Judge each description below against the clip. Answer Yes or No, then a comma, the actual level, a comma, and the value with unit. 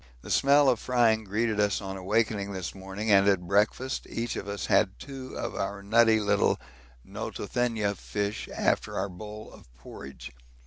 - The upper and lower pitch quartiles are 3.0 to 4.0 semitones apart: No, narrow, 2.6 semitones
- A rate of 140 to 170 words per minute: Yes, average, 165 wpm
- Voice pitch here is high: No, low, 105 Hz